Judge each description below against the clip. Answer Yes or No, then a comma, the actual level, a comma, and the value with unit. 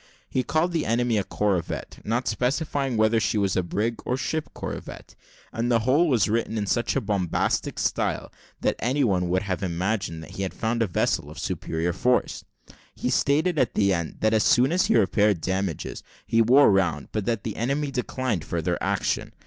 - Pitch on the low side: Yes, low, 110 Hz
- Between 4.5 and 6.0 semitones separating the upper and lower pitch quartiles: Yes, average, 4.8 semitones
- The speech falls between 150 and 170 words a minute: No, average, 190 wpm